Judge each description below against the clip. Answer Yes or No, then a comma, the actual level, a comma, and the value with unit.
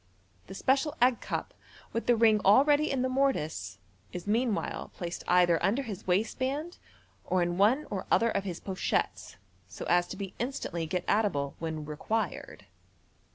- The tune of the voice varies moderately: No, wide, 6.4 semitones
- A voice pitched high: Yes, high, 205 Hz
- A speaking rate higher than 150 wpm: Yes, average, 165 wpm